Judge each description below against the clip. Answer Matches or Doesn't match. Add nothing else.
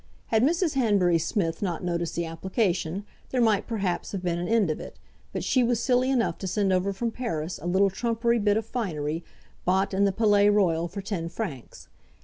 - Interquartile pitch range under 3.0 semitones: Doesn't match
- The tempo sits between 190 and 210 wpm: Matches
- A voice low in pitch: Doesn't match